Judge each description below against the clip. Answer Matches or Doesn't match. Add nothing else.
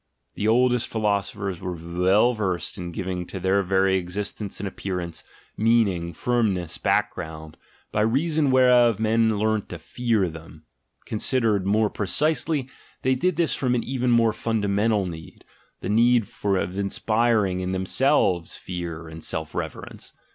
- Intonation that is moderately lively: Matches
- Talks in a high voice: Doesn't match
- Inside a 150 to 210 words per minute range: Doesn't match